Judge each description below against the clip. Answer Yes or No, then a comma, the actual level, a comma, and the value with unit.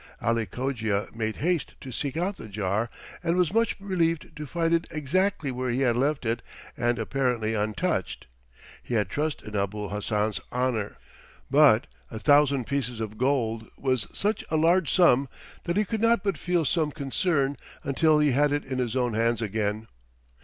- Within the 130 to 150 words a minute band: No, average, 175 wpm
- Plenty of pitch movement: Yes, wide, 5.9 semitones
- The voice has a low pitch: Yes, low, 130 Hz